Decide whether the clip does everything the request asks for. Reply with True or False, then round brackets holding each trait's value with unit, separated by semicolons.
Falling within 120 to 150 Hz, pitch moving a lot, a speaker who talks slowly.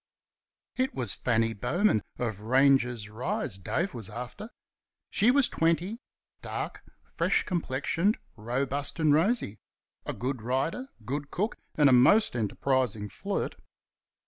True (135 Hz; 7.0 semitones; 120 wpm)